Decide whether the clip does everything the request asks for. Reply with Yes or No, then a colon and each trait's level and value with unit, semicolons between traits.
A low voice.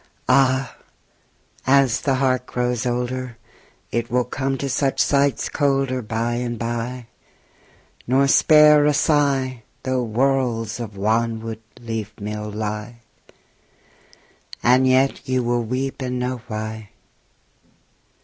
Yes: low, 125 Hz